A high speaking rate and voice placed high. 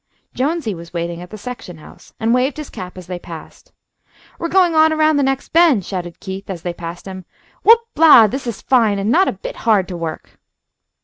Yes: fast, 210 wpm; high, 215 Hz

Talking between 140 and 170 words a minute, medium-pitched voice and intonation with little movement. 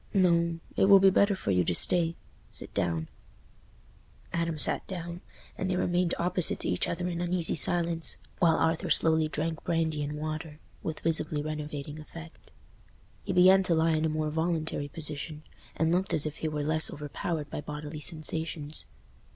Yes: average, 165 wpm; medium, 160 Hz; narrow, 2.1 semitones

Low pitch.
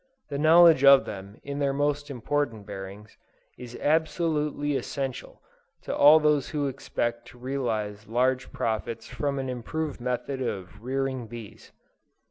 Yes: low, 130 Hz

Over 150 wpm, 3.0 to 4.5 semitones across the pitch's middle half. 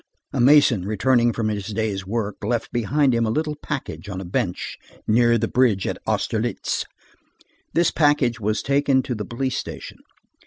Yes: average, 165 wpm; average, 3.8 semitones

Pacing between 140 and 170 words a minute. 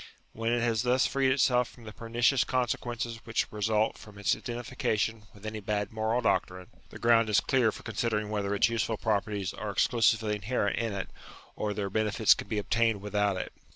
No: average, 190 wpm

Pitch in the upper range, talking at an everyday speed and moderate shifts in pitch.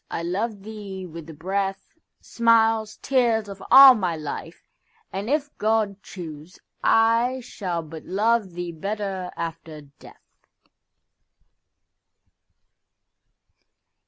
No: high, 200 Hz; slow, 95 wpm; average, 4.5 semitones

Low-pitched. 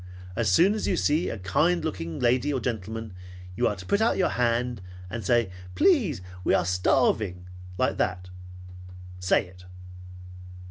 Yes: low, 115 Hz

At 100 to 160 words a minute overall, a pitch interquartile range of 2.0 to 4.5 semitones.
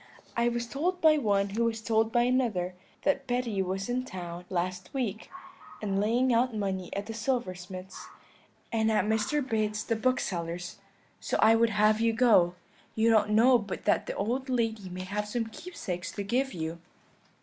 No: average, 175 wpm; average, 3.8 semitones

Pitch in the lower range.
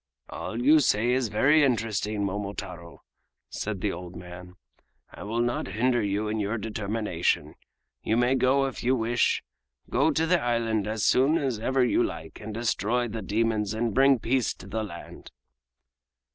Yes: low, 110 Hz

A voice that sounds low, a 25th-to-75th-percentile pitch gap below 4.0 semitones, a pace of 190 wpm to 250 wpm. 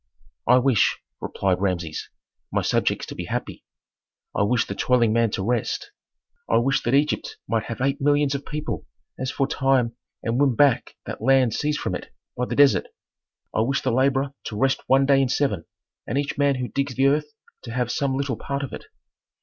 Yes: low, 130 Hz; average, 3.1 semitones; average, 200 wpm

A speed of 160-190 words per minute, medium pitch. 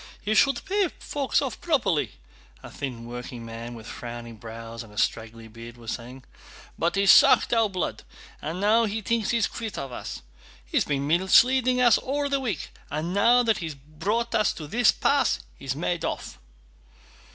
Yes: average, 175 wpm; medium, 175 Hz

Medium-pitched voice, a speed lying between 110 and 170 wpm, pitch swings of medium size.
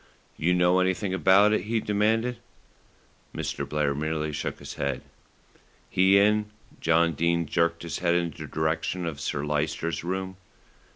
No: very low, 85 Hz; average, 150 wpm; average, 3.3 semitones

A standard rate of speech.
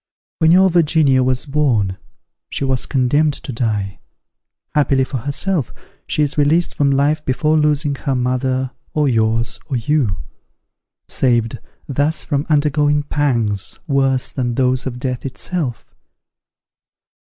No: slow, 130 wpm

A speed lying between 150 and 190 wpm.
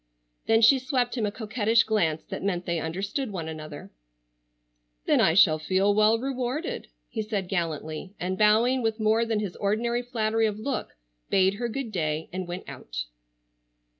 Yes: average, 165 wpm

